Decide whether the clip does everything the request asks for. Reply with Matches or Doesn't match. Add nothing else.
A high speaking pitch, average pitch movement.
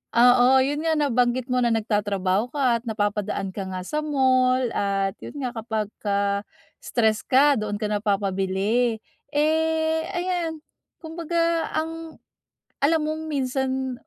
Doesn't match